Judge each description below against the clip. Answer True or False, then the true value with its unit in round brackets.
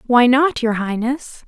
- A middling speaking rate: True (165 wpm)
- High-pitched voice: True (245 Hz)